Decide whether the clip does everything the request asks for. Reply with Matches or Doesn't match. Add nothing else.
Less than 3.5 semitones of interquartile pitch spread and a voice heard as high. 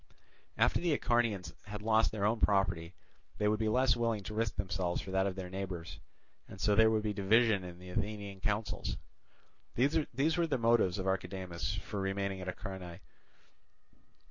Doesn't match